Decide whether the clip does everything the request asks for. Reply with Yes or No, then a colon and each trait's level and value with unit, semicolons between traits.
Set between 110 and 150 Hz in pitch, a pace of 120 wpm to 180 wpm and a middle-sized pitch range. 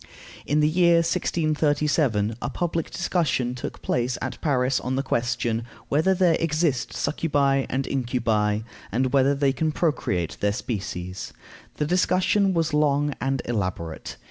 Yes: medium, 140 Hz; average, 140 wpm; average, 4.7 semitones